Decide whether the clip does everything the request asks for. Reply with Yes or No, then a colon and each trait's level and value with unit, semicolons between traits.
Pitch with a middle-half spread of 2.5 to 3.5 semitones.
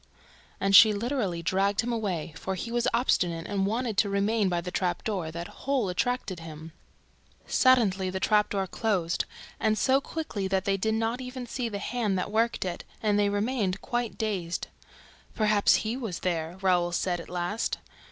No: average, 3.9 semitones